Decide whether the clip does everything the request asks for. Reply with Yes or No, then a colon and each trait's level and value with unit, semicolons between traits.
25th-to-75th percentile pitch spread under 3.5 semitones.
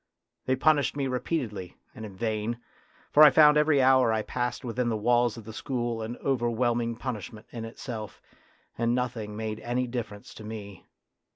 Yes: narrow, 2.5 semitones